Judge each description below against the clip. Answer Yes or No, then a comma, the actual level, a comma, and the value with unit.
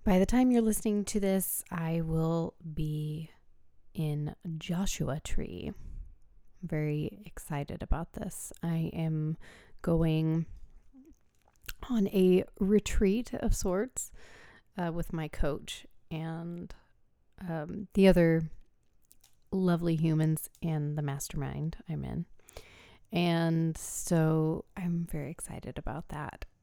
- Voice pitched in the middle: Yes, medium, 165 Hz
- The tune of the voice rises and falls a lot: No, average, 3.1 semitones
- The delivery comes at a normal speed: No, slow, 110 wpm